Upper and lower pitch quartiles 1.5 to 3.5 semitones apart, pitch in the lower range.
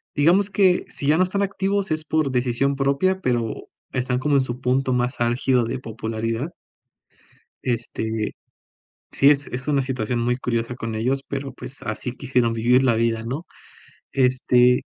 Yes: average, 2.9 semitones; low, 130 Hz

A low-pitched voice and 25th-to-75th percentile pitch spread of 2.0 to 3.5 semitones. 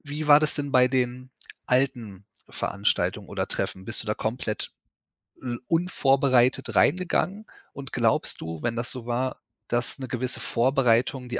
Yes: low, 125 Hz; narrow, 2.6 semitones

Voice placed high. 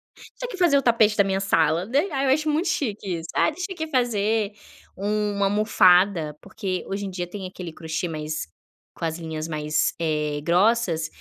Yes: high, 200 Hz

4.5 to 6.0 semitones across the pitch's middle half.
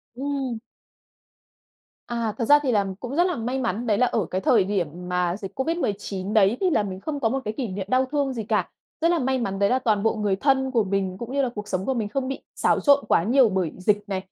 Yes: average, 5.0 semitones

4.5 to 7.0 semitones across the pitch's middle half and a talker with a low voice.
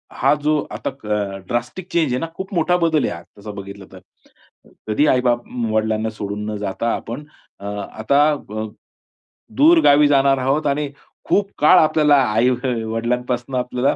Yes: wide, 5.5 semitones; low, 125 Hz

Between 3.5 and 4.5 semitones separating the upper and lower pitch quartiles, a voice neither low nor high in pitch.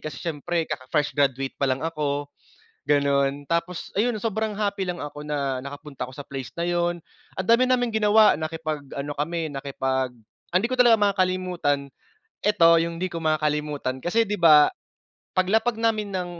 No: average, 4.9 semitones; medium, 165 Hz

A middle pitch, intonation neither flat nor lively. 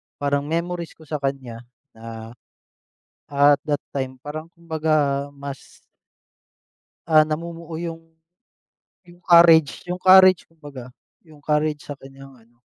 Yes: medium, 150 Hz; average, 3.0 semitones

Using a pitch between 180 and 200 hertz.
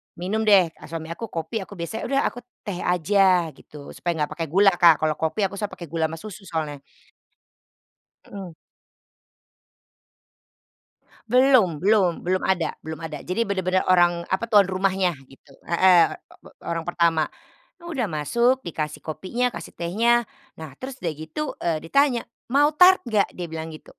Yes: medium, 185 Hz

